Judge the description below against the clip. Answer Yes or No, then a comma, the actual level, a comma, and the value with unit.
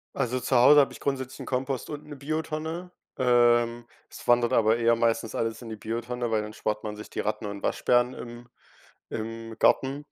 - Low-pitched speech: Yes, low, 120 Hz